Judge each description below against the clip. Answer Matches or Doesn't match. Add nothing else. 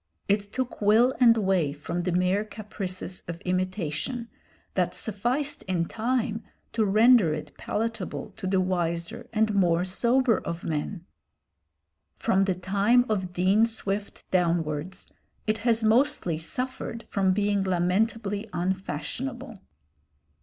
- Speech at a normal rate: Doesn't match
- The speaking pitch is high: Matches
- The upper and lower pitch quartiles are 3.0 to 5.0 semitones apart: Matches